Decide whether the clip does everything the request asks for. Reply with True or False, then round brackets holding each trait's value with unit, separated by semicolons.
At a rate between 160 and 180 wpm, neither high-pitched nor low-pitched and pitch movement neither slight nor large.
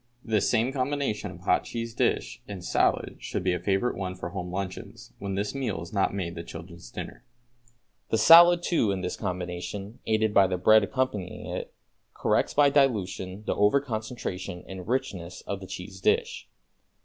False (175 wpm; 100 Hz; 4.1 semitones)